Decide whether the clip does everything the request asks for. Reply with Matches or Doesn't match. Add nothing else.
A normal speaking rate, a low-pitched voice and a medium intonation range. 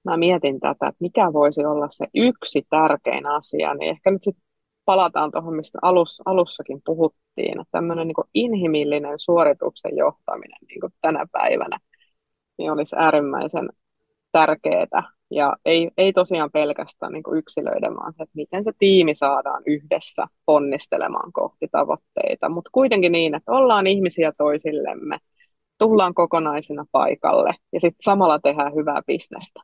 Doesn't match